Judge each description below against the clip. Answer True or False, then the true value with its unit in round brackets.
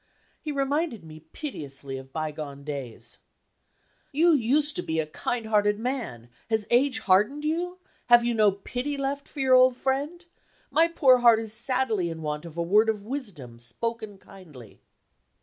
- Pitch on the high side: True (225 Hz)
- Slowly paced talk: False (165 wpm)